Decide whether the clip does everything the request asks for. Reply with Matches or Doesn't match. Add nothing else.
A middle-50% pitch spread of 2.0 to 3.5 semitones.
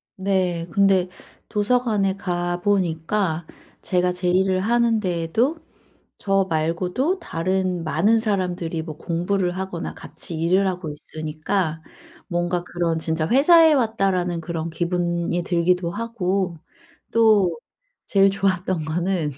Matches